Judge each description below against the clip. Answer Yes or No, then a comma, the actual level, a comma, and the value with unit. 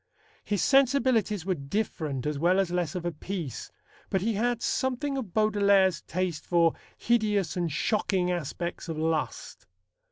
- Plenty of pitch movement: No, average, 4.4 semitones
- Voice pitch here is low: No, medium, 185 Hz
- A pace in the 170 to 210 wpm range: No, average, 150 wpm